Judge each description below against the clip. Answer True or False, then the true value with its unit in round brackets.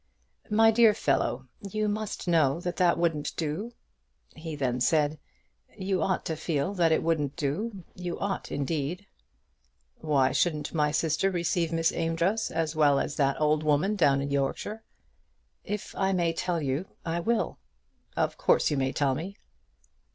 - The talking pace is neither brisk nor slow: True (160 wpm)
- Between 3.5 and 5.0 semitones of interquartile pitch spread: True (4.3 semitones)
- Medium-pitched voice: True (165 Hz)